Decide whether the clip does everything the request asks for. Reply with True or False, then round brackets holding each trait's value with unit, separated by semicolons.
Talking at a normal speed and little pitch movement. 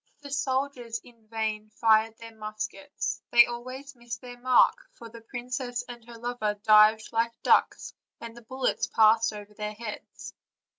True (160 wpm; 2.0 semitones)